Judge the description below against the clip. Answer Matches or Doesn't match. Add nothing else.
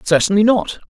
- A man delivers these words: Doesn't match